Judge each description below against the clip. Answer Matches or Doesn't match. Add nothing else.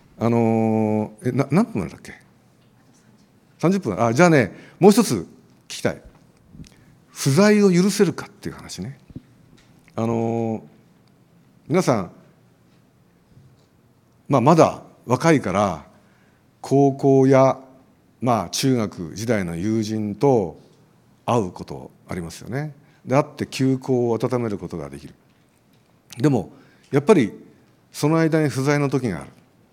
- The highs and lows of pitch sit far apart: Doesn't match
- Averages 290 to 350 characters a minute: Doesn't match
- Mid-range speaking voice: Doesn't match